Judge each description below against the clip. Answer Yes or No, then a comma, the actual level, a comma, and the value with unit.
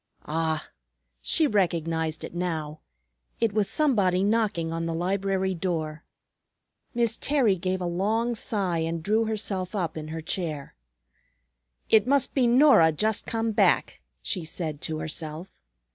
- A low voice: No, medium, 185 Hz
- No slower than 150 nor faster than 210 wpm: No, average, 140 wpm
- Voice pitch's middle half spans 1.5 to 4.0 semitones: No, average, 5.1 semitones